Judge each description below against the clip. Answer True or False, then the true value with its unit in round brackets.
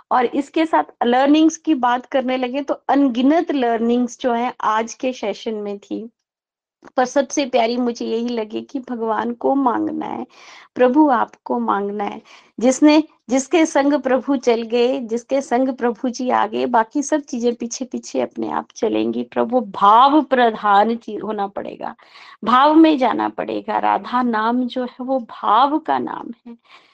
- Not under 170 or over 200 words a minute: False (155 wpm)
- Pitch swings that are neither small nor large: True (3.7 semitones)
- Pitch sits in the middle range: False (250 Hz)